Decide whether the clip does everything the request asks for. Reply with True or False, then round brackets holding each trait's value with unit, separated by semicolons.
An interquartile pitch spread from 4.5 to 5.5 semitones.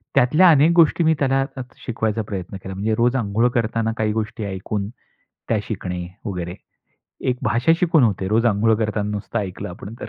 False (3.6 semitones)